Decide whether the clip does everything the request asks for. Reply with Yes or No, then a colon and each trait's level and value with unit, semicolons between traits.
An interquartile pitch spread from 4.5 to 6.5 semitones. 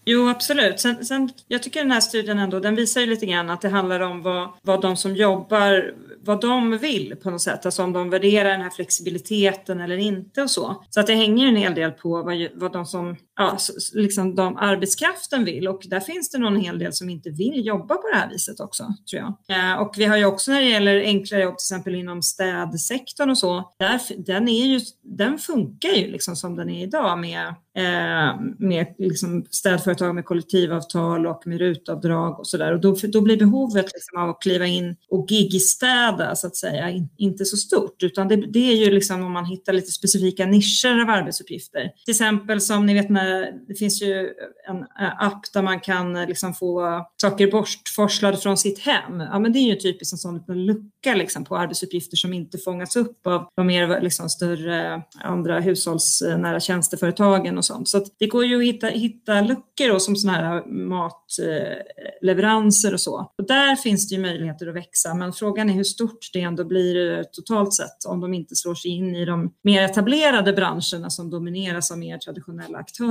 No: average, 2.9 semitones